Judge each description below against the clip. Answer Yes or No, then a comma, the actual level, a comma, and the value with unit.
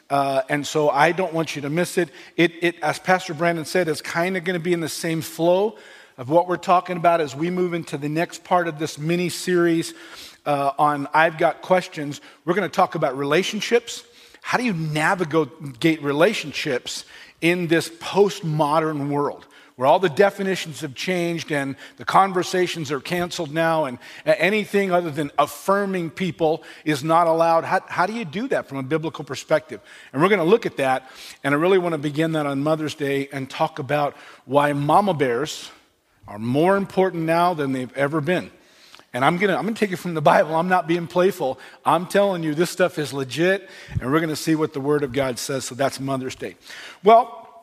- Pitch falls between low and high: Yes, medium, 165 Hz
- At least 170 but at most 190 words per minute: No, fast, 205 wpm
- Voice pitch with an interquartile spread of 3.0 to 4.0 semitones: Yes, average, 3.5 semitones